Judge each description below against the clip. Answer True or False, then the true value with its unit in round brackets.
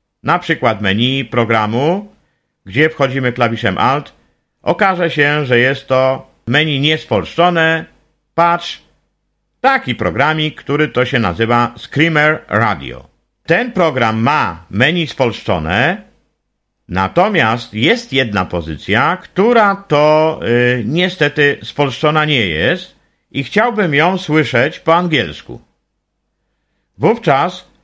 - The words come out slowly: True (100 wpm)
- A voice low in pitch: False (145 Hz)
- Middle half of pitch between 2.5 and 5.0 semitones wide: False (5.4 semitones)